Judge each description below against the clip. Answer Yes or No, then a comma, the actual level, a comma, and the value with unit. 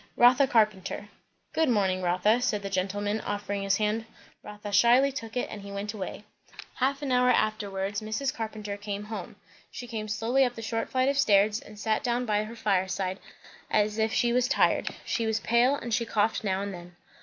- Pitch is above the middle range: Yes, high, 215 Hz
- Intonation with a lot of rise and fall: No, average, 2.8 semitones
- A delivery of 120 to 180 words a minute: No, average, 195 wpm